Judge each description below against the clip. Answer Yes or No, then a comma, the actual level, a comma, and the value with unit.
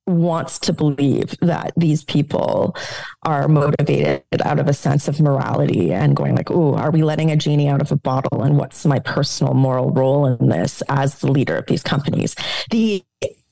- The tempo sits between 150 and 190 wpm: Yes, average, 185 wpm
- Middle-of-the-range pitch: Yes, medium, 145 Hz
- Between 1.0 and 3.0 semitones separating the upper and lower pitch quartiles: Yes, narrow, 2.4 semitones